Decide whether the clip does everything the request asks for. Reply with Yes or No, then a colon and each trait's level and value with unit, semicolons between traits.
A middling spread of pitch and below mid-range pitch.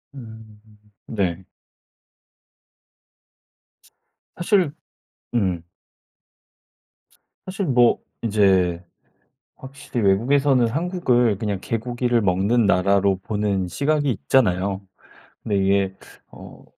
Yes: average, 4.9 semitones; low, 110 Hz